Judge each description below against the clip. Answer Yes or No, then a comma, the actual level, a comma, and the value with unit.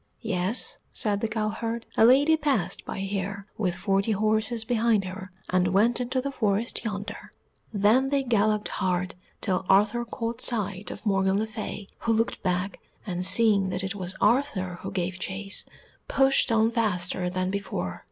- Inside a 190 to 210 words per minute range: No, average, 160 wpm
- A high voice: Yes, high, 205 Hz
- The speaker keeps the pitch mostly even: No, average, 3.4 semitones